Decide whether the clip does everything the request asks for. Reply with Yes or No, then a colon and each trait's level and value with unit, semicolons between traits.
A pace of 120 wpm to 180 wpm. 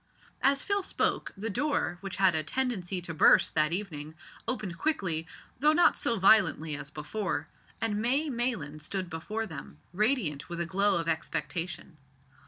Yes: average, 160 wpm